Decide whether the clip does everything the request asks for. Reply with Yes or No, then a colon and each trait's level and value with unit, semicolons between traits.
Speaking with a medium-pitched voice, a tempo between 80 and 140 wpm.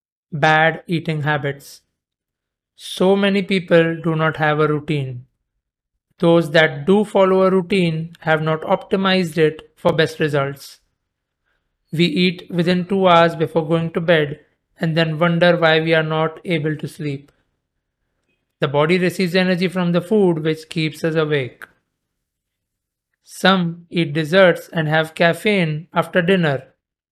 Yes: medium, 165 Hz; slow, 135 wpm